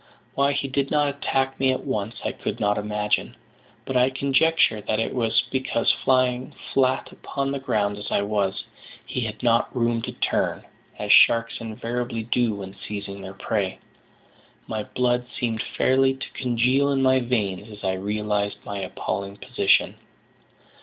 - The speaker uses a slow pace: No, average, 160 wpm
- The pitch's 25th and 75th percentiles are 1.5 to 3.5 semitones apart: No, average, 4.1 semitones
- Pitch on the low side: Yes, low, 115 Hz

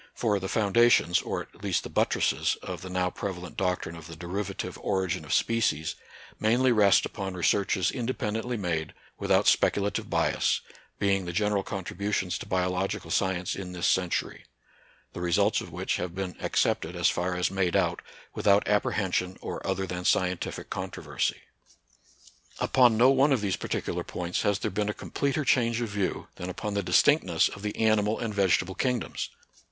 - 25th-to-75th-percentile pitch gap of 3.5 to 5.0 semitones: No, average, 2.8 semitones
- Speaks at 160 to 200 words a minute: Yes, average, 170 wpm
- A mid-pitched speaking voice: No, very low, 95 Hz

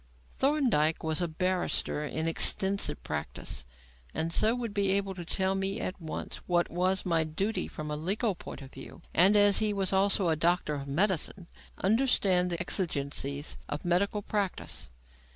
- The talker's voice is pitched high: No, medium, 180 Hz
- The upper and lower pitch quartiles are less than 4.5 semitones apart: Yes, average, 3.9 semitones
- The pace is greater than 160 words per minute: Yes, average, 170 wpm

